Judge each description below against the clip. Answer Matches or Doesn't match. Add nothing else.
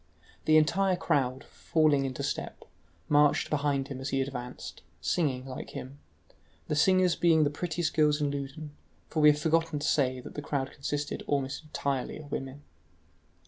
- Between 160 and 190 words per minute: Matches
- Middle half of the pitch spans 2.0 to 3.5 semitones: Matches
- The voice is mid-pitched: Matches